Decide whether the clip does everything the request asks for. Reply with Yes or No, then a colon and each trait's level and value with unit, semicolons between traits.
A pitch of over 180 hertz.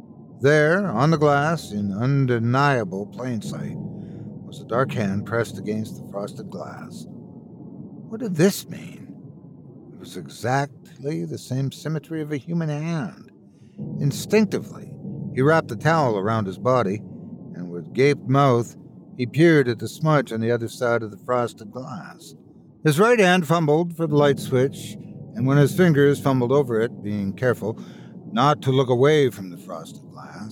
No: medium, 140 Hz